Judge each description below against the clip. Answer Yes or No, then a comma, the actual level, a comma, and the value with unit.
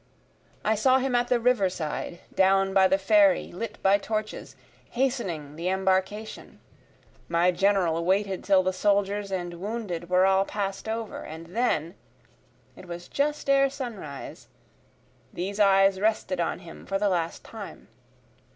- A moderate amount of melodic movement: Yes, average, 3.3 semitones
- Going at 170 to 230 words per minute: No, average, 145 wpm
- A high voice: Yes, high, 195 Hz